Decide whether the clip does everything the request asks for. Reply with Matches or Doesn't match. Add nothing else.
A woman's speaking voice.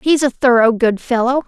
Matches